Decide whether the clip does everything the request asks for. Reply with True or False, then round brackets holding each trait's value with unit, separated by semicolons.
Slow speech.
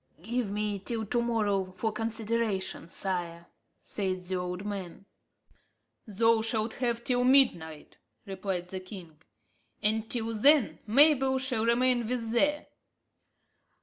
True (120 wpm)